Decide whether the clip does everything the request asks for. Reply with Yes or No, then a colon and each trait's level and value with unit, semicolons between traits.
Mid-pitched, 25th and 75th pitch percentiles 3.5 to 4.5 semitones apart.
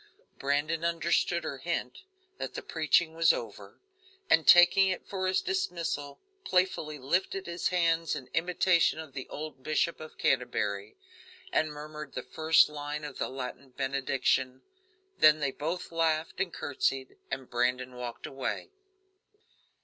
Yes: medium, 155 Hz; average, 4.1 semitones